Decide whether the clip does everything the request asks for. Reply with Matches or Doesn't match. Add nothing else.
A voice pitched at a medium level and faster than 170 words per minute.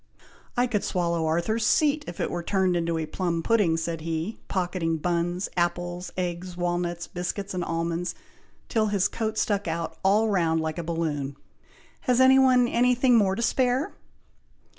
Doesn't match